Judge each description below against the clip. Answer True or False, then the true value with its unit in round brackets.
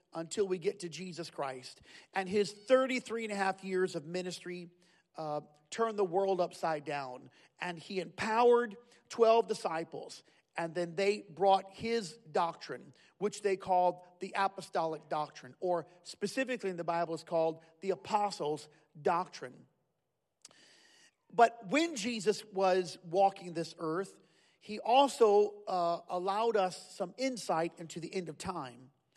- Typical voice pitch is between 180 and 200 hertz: True (185 Hz)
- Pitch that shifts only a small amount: False (3.7 semitones)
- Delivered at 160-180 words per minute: False (140 wpm)